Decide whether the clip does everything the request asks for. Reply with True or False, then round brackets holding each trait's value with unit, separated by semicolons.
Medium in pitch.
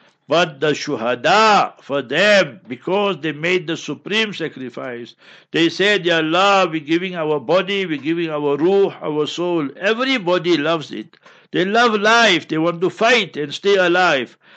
True (170 Hz)